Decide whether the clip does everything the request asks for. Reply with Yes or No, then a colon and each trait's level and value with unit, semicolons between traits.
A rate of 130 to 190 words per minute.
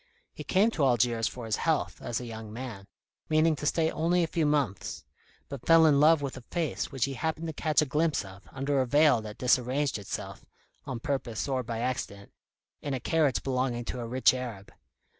No: fast, 205 wpm